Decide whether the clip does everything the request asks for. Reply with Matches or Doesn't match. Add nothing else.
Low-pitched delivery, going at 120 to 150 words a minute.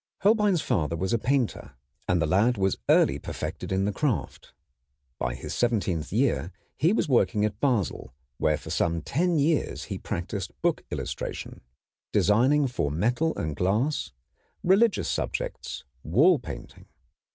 Matches